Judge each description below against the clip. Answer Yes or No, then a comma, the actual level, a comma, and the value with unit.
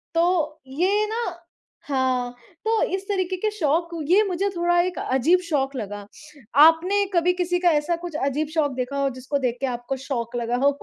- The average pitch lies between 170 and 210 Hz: No, very high, 320 Hz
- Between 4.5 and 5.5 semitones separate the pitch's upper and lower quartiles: Yes, average, 5.2 semitones